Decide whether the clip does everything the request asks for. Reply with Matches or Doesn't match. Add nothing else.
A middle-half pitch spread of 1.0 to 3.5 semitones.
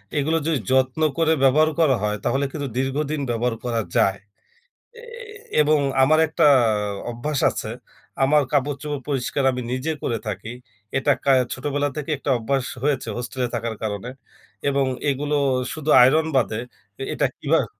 Matches